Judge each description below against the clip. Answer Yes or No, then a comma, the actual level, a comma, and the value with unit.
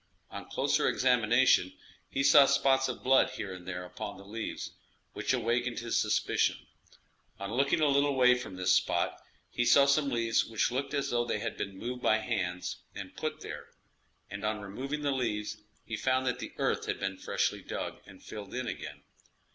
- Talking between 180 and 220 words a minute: Yes, average, 185 wpm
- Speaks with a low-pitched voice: Yes, low, 120 Hz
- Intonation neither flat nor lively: Yes, average, 3.9 semitones